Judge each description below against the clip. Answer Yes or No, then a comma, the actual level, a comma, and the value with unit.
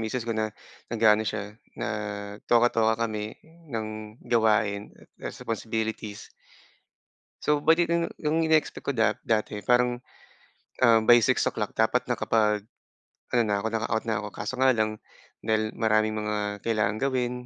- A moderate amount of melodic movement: No, narrow, 2.0 semitones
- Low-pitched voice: Yes, low, 110 Hz